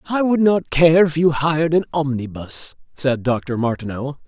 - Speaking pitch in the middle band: Yes, medium, 150 Hz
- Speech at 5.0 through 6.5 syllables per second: No, 4.5 syllables/s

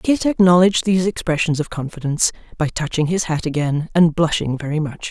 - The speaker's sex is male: No, female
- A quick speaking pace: No, average, 175 wpm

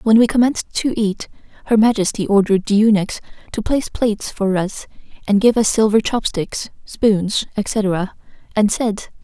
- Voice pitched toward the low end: No, high, 215 Hz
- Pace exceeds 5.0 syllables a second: No, 4.8 syllables/s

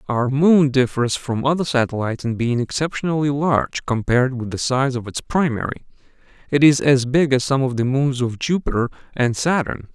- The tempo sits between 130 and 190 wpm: Yes, average, 180 wpm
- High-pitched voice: No, low, 135 Hz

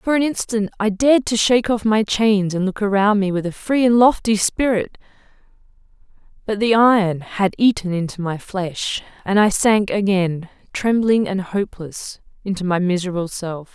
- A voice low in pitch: No, high, 205 Hz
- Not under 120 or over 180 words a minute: Yes, average, 170 wpm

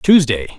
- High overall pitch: No, medium, 140 Hz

